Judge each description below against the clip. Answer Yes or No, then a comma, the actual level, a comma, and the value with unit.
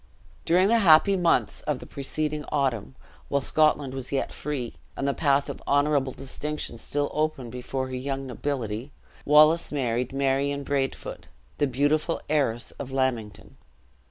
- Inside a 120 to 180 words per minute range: Yes, average, 145 wpm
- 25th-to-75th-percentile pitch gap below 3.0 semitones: Yes, narrow, 2.4 semitones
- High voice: No, medium, 140 Hz